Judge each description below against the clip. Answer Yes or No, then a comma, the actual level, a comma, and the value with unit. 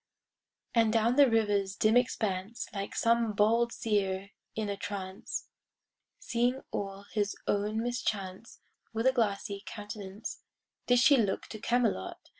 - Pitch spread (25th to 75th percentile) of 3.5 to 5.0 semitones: No, average, 2.7 semitones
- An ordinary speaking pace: No, slow, 130 wpm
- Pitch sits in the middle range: No, high, 215 Hz